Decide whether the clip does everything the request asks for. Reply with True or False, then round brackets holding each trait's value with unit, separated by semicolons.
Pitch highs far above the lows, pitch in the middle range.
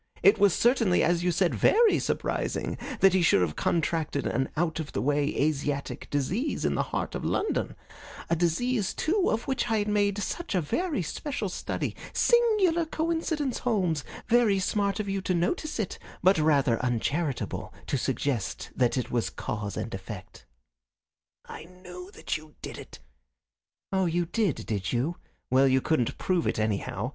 True (7.5 semitones; 180 Hz)